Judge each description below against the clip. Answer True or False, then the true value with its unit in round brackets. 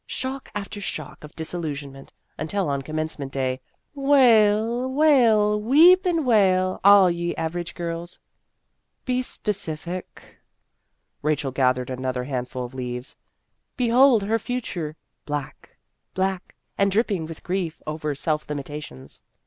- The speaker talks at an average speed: False (120 wpm)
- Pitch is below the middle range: False (175 Hz)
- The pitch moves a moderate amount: False (7.1 semitones)